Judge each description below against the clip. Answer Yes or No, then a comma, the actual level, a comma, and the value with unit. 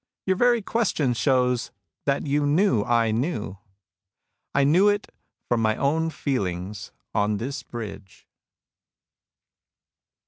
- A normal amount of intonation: No, wide, 6.7 semitones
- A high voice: No, low, 130 Hz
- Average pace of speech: No, slow, 110 wpm